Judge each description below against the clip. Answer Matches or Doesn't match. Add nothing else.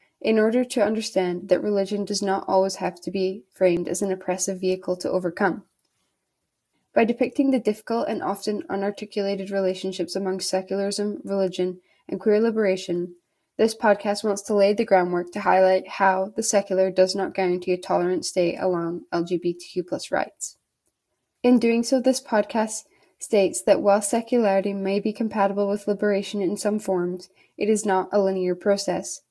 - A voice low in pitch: Doesn't match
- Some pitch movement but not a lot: Doesn't match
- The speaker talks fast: Doesn't match